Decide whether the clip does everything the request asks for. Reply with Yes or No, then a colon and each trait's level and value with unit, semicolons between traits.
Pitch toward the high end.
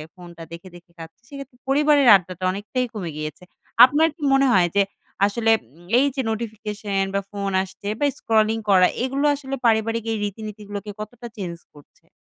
Yes: high, 210 Hz